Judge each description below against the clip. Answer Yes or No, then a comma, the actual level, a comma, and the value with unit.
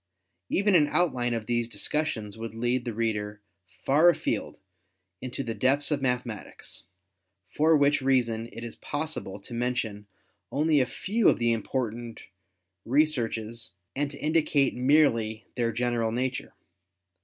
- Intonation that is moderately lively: Yes, average, 4.1 semitones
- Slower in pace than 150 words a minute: Yes, slow, 135 wpm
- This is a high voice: No, low, 125 Hz